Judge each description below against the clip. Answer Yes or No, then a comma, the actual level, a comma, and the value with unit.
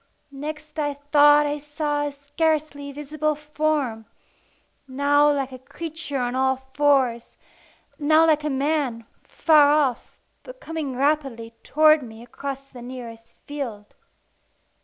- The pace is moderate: No, slow, 125 wpm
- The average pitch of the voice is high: Yes, very high, 290 Hz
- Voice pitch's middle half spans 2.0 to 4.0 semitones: Yes, narrow, 2.5 semitones